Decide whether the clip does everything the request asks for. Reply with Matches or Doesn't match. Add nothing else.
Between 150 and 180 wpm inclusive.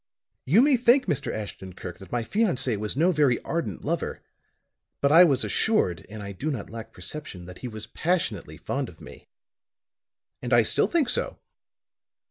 Matches